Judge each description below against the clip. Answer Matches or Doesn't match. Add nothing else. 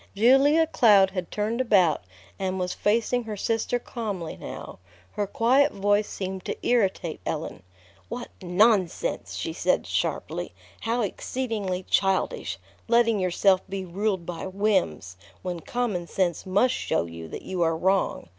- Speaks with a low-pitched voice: Doesn't match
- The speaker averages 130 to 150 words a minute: Matches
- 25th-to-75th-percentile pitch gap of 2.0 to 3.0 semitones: Doesn't match